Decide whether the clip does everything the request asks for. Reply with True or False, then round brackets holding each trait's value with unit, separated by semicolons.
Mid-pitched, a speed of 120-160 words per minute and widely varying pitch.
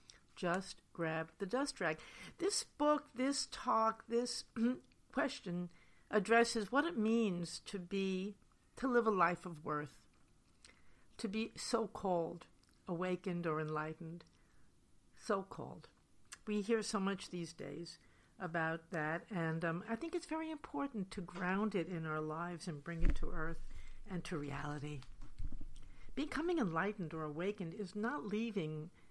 True (180 Hz; 140 wpm; 5.7 semitones)